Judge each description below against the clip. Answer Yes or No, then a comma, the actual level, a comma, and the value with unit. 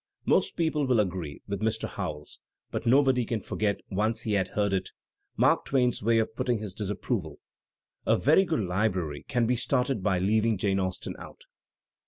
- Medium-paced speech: Yes, average, 175 wpm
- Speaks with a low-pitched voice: Yes, low, 110 Hz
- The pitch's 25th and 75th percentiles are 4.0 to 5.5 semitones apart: Yes, average, 4.3 semitones